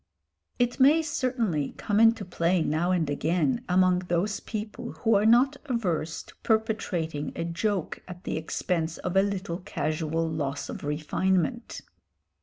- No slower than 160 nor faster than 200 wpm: No, average, 145 wpm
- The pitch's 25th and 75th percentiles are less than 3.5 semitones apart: No, average, 5.3 semitones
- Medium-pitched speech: Yes, medium, 180 Hz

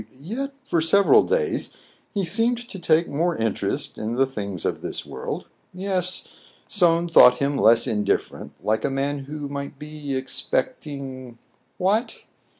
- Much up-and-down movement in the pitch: Yes, wide, 5.8 semitones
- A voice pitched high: No, medium, 150 Hz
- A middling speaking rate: Yes, average, 150 wpm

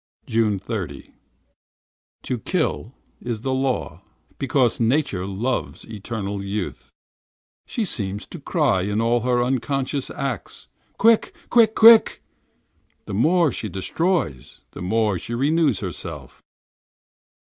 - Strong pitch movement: Yes, wide, 5.8 semitones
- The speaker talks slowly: Yes, slow, 115 wpm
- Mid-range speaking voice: No, low, 120 Hz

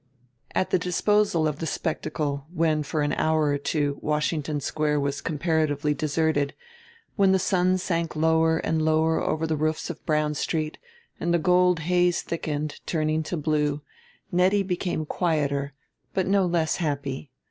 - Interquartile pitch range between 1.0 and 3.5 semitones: Yes, narrow, 2.4 semitones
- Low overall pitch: No, medium, 155 Hz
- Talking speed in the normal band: Yes, average, 155 wpm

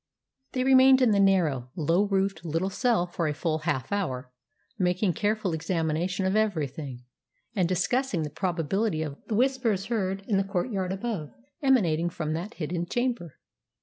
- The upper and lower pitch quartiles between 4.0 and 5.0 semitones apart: Yes, average, 4.7 semitones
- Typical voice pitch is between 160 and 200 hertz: Yes, medium, 185 Hz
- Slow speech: No, average, 155 wpm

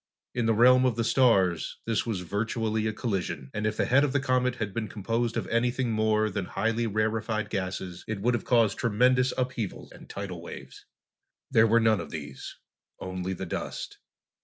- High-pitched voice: No, low, 110 Hz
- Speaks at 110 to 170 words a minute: No, average, 185 wpm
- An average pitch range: Yes, average, 3.4 semitones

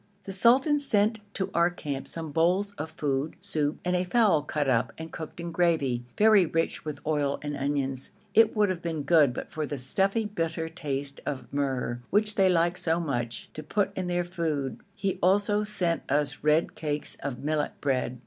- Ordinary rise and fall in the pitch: Yes, average, 4.7 semitones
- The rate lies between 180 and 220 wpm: Yes, average, 190 wpm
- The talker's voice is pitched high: No, medium, 160 Hz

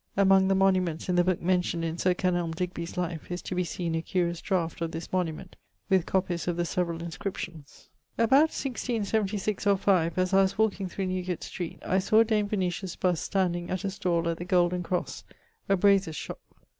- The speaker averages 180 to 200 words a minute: Yes, average, 195 wpm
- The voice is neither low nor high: Yes, medium, 180 Hz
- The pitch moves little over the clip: Yes, narrow, 2.1 semitones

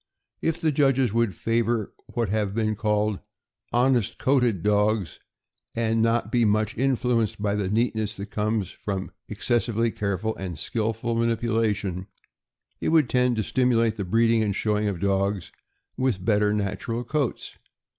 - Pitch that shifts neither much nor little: No, narrow, 2.3 semitones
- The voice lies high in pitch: No, low, 110 Hz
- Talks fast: No, average, 145 wpm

